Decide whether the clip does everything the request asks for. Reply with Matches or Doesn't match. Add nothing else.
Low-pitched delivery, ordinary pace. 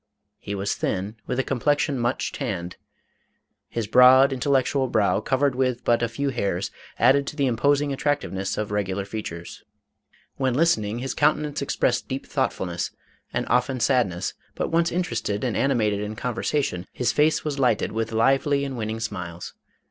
Matches